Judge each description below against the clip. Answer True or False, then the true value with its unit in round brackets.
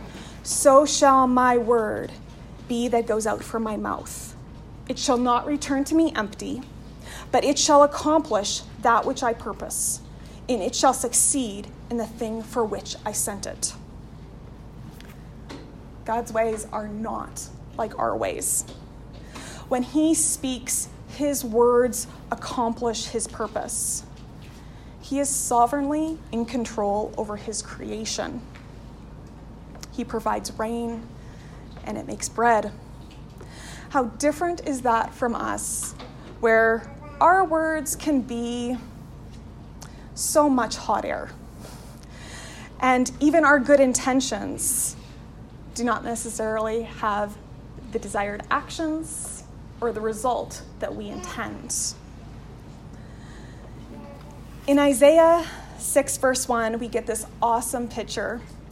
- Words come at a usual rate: False (115 wpm)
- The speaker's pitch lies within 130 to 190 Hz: False (245 Hz)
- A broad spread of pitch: False (3.9 semitones)